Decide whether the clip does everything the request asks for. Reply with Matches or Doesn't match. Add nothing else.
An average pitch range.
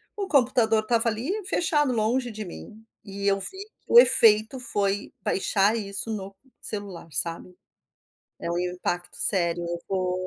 Matches